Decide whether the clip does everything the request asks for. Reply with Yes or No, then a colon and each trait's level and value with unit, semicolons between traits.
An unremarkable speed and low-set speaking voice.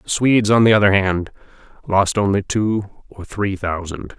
Yes: average, 170 wpm; low, 100 Hz